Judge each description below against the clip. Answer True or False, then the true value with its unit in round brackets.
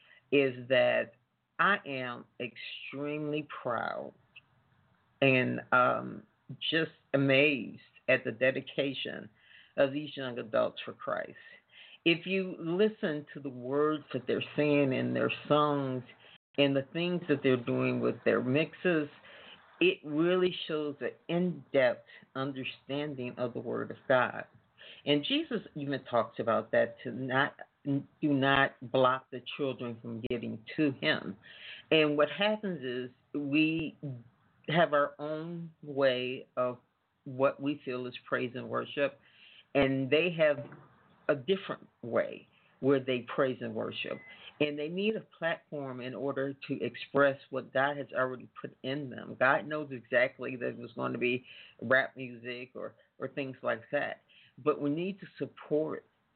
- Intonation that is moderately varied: True (3.0 semitones)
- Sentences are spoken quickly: False (145 wpm)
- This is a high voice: False (140 Hz)